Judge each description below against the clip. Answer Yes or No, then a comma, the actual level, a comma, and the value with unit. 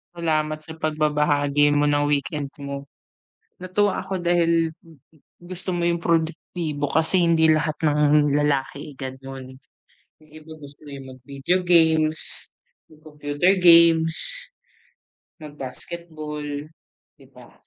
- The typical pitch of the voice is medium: Yes, medium, 155 Hz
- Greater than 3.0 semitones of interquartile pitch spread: No, narrow, 2.5 semitones